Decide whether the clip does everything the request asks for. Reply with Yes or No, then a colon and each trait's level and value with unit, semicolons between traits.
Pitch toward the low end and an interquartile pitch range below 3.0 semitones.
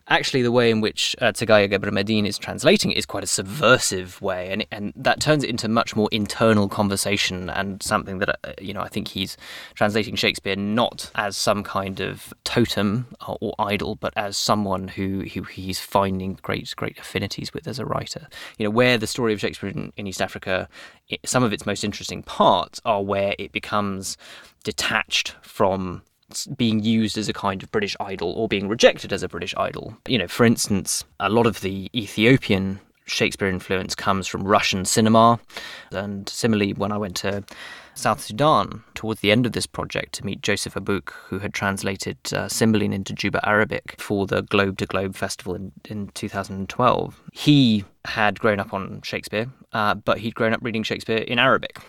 Yes: low, 100 Hz; narrow, 2.5 semitones